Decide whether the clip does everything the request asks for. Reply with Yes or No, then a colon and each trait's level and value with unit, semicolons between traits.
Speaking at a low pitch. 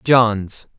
Yes: low, 110 Hz